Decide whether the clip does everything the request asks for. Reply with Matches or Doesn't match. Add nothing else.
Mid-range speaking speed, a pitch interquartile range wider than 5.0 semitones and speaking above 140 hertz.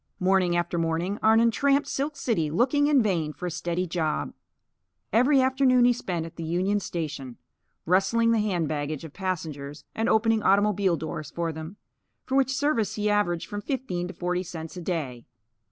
Matches